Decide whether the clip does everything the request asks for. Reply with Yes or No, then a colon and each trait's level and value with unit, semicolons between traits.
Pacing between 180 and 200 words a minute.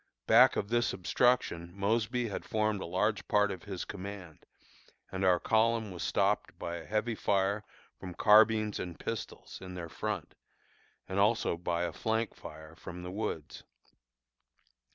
No: average, 155 wpm